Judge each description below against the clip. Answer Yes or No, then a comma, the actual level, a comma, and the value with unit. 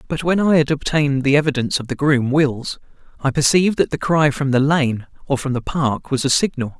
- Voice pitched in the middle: Yes, medium, 145 Hz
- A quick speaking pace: Yes, fast, 230 wpm